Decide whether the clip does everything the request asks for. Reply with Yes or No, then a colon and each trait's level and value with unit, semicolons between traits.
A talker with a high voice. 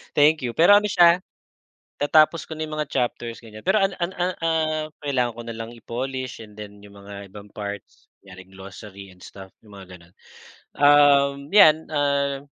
No: low, 130 Hz